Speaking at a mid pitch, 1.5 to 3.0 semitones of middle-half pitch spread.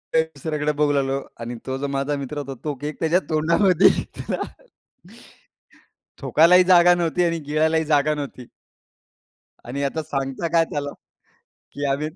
Yes: medium, 150 Hz; narrow, 2.5 semitones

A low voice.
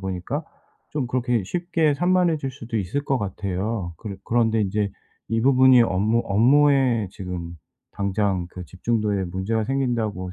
Yes: low, 110 Hz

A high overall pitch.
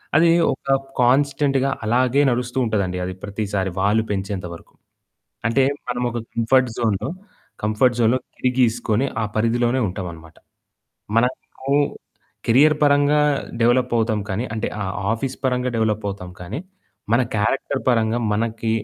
No: low, 115 Hz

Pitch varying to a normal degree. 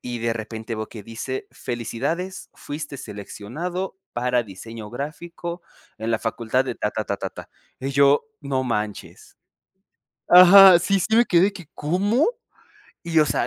No: wide, 7.3 semitones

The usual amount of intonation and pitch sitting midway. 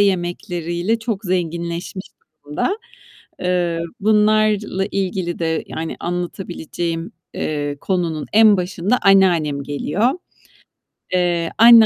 Yes: average, 3.2 semitones; medium, 180 Hz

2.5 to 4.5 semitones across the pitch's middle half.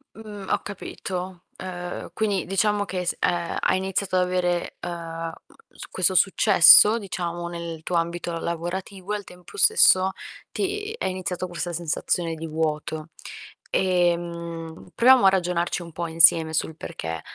No: narrow, 2.1 semitones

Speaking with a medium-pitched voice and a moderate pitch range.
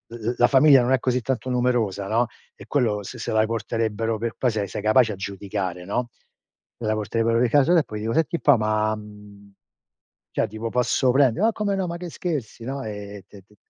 No: low, 115 Hz; average, 3.5 semitones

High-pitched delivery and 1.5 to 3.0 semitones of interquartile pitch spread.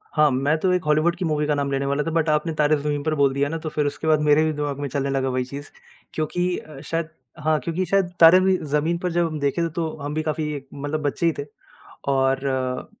No: medium, 150 Hz; narrow, 2.4 semitones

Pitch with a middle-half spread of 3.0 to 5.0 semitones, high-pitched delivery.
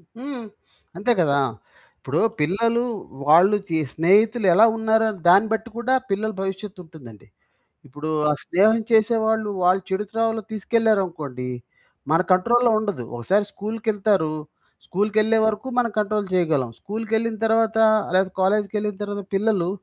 Yes: average, 3.5 semitones; high, 210 Hz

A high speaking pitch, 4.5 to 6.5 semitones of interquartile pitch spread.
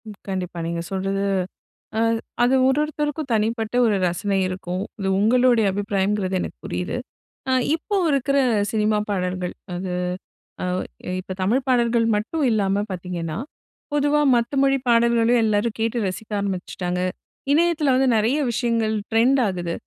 Yes: high, 220 Hz; average, 4.9 semitones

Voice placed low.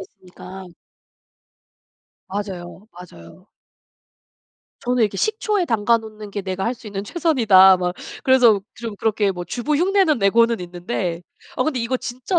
No: high, 215 Hz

